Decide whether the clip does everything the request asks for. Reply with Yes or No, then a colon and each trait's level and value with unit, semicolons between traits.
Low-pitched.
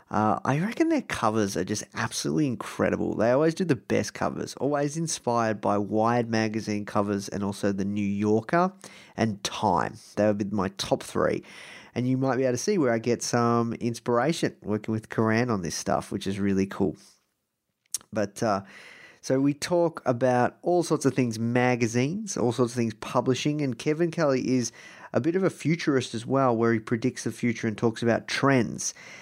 Yes: low, 120 Hz